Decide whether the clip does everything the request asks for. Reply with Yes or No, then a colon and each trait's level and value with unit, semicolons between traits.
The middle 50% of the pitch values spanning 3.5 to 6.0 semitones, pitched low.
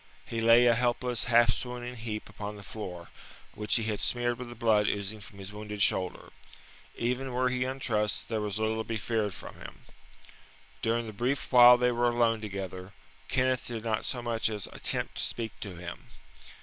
No: narrow, 2.5 semitones; low, 115 Hz